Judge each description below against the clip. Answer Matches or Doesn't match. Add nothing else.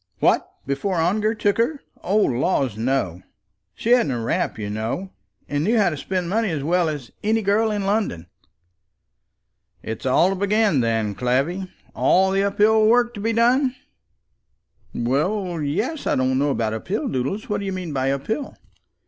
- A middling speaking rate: Matches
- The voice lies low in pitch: Doesn't match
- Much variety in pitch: Matches